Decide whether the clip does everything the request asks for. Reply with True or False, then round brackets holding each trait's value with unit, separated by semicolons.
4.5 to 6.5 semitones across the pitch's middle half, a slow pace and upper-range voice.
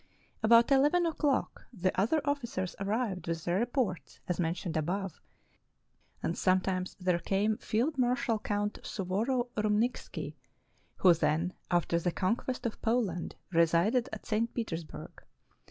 True (5.2 semitones; 130 wpm; 205 Hz)